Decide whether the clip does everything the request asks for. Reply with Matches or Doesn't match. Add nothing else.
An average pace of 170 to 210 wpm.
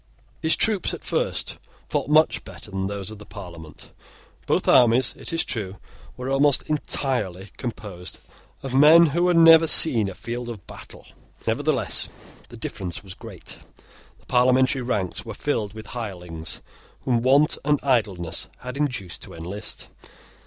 Doesn't match